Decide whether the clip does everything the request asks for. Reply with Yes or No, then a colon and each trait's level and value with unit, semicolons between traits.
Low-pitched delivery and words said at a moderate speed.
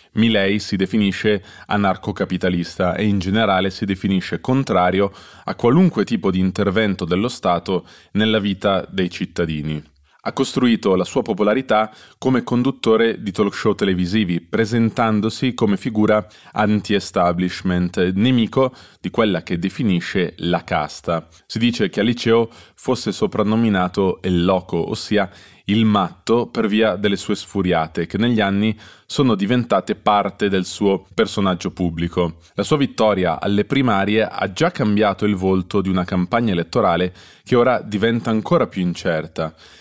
Yes: low, 100 Hz; average, 135 wpm